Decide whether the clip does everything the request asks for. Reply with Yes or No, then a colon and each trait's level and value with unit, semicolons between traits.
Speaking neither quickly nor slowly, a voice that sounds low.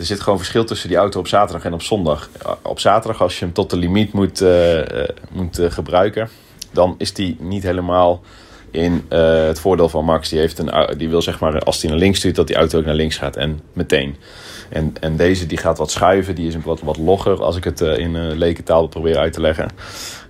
No: fast, 240 wpm; very low, 85 Hz